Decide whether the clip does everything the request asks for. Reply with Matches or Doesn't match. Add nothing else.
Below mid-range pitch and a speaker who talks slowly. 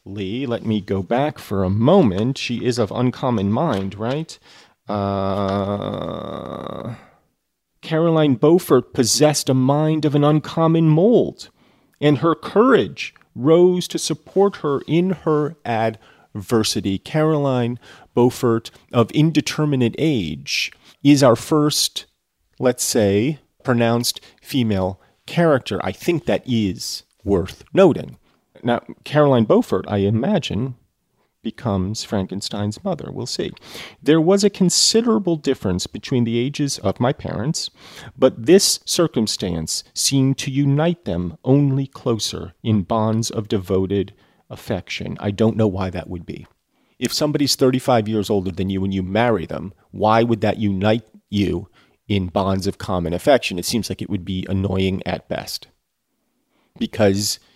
Matches